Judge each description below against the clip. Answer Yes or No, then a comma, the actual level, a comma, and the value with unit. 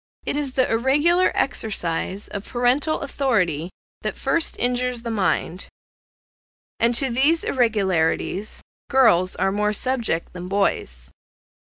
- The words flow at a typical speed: No, slow, 120 wpm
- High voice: Yes, high, 230 Hz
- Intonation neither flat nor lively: No, wide, 5.7 semitones